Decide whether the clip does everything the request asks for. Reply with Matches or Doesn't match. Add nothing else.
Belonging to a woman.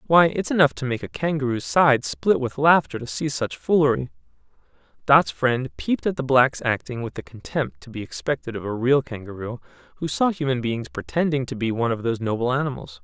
Doesn't match